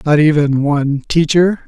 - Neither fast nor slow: Yes, average, 145 wpm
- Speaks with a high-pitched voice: No, medium, 150 Hz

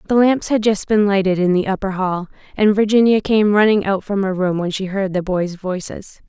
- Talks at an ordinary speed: No, fast, 230 wpm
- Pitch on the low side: No, high, 200 Hz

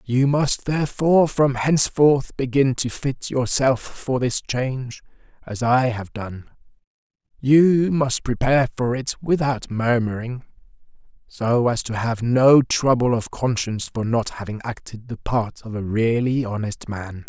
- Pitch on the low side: Yes, low, 125 Hz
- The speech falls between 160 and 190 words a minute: No, average, 145 wpm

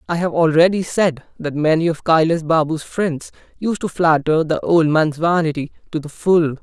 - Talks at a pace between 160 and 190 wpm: Yes, average, 180 wpm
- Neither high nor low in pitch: Yes, medium, 160 Hz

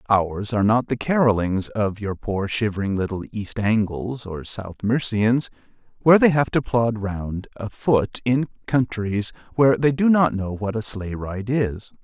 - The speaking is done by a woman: No, male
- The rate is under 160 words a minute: No, average, 170 wpm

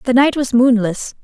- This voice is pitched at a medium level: No, high, 245 Hz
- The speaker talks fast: No, average, 195 wpm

